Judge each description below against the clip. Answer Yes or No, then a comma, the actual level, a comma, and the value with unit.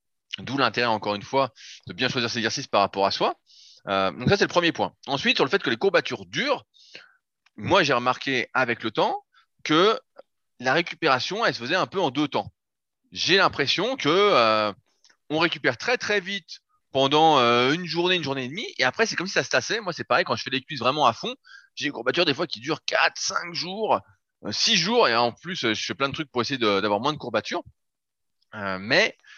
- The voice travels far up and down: Yes, wide, 8.2 semitones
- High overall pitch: No, medium, 140 Hz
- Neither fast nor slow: No, fast, 225 wpm